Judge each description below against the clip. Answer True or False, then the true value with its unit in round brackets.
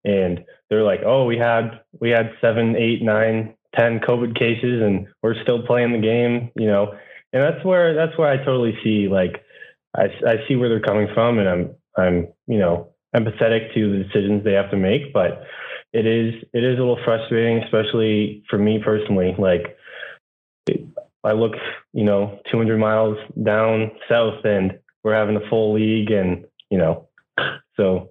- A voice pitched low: True (110 Hz)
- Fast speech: False (180 wpm)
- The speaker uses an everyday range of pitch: False (1.9 semitones)